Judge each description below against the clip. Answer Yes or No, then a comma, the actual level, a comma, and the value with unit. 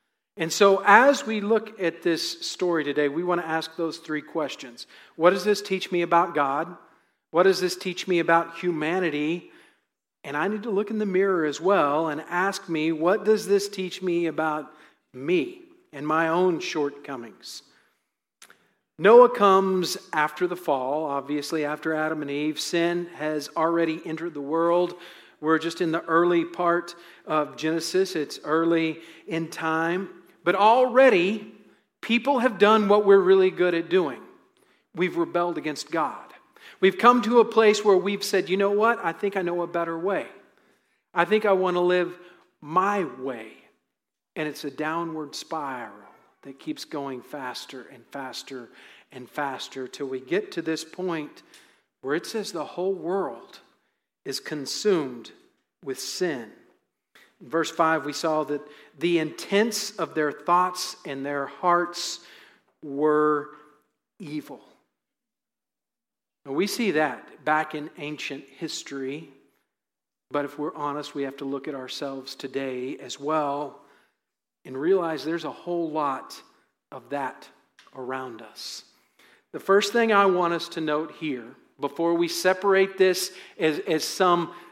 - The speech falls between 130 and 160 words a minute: Yes, average, 150 wpm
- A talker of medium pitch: Yes, medium, 170 Hz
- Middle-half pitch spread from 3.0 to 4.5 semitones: Yes, average, 3.7 semitones